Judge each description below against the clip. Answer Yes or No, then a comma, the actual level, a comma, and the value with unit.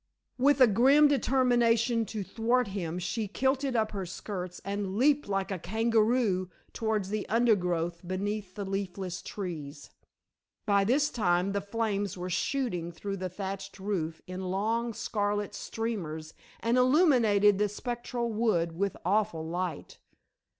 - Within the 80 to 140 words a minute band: Yes, slow, 135 wpm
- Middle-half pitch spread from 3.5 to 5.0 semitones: Yes, average, 3.9 semitones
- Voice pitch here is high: Yes, high, 205 Hz